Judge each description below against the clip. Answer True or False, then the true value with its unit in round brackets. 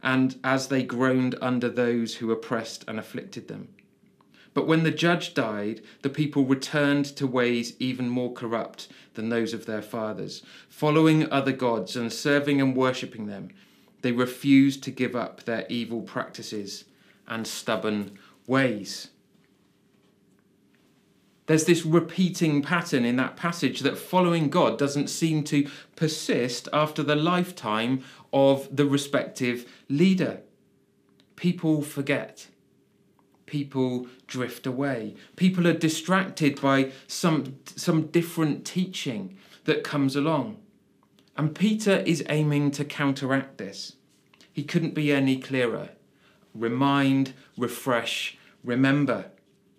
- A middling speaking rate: False (120 wpm)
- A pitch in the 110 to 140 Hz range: True (135 Hz)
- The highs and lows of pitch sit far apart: False (3.6 semitones)